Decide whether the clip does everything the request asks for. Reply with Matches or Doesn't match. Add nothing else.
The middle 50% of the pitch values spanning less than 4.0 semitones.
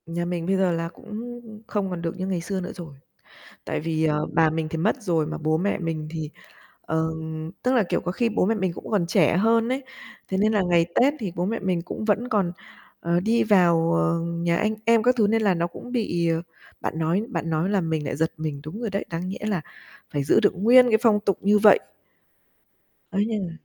Doesn't match